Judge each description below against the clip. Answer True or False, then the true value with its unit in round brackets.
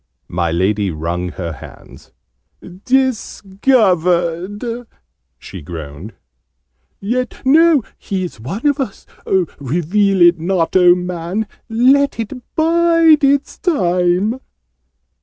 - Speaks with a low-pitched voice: False (190 Hz)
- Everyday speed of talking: False (100 wpm)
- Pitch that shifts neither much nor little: False (7.5 semitones)